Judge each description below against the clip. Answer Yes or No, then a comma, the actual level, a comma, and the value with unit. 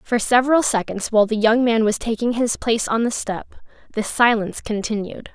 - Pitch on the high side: Yes, high, 225 Hz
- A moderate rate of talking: Yes, average, 190 wpm